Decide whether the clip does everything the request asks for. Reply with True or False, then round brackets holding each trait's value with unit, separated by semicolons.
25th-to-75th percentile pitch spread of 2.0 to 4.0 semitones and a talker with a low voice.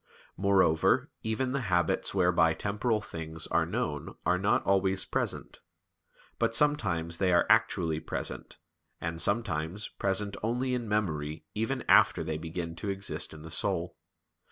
False (4.6 semitones; 95 Hz)